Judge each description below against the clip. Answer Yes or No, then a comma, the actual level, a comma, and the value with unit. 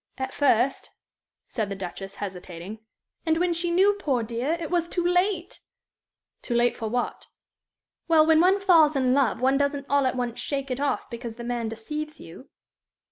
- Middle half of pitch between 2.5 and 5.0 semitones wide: No, wide, 5.6 semitones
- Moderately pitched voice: No, very high, 275 Hz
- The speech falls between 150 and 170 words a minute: No, average, 180 wpm